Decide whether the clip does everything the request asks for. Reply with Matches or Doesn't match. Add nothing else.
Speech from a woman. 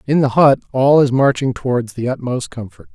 Doesn't match